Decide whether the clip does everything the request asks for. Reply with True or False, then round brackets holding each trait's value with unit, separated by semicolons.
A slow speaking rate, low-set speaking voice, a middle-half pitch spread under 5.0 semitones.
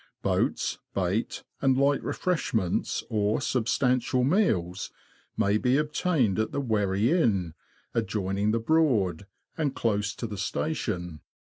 False (125 wpm; 110 Hz; 5.4 semitones)